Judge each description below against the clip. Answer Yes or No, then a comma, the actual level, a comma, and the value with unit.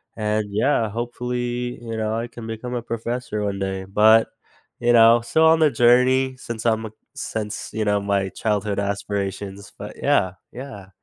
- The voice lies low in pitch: Yes, low, 110 Hz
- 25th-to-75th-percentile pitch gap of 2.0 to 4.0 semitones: Yes, average, 2.9 semitones